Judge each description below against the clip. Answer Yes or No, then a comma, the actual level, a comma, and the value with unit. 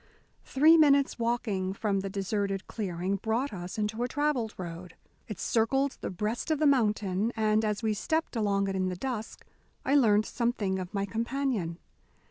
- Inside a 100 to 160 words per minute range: No, average, 170 wpm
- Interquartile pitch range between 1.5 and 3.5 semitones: No, average, 4.0 semitones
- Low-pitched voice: No, high, 215 Hz